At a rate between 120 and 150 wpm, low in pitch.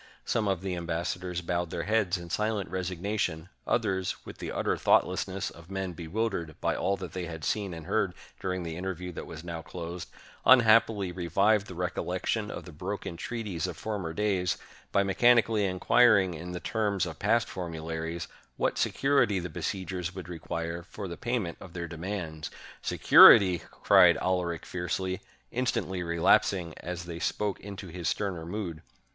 No: average, 165 wpm; very low, 90 Hz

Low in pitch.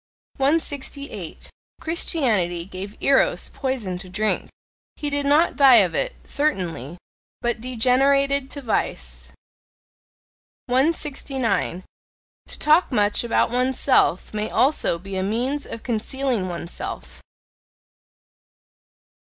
No: very high, 250 Hz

